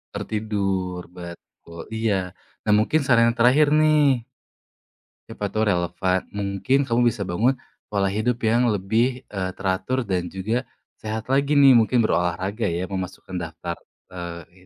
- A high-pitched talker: No, low, 105 Hz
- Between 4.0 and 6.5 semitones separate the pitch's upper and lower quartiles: Yes, average, 4.6 semitones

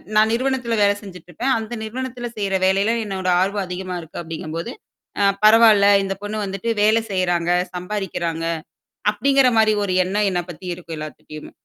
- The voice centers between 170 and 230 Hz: Yes, high, 200 Hz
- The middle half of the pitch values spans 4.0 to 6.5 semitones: No, average, 3.6 semitones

